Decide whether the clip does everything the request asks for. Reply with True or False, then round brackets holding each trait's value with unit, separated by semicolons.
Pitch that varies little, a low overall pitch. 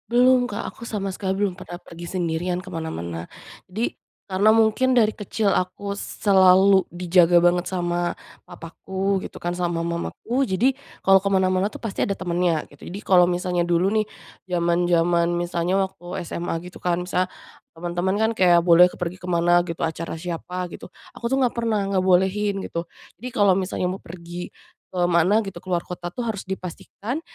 False (2.3 semitones; 180 Hz)